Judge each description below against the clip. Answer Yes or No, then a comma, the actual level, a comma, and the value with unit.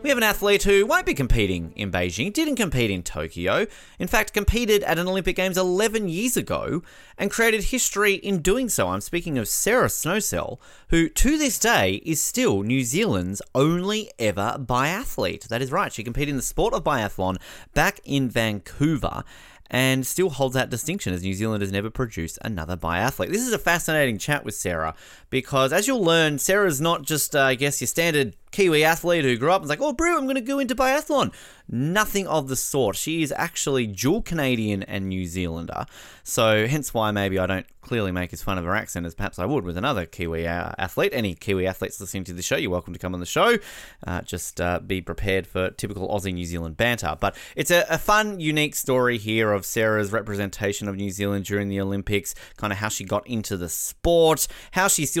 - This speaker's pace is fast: Yes, fast, 210 wpm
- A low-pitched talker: Yes, low, 125 Hz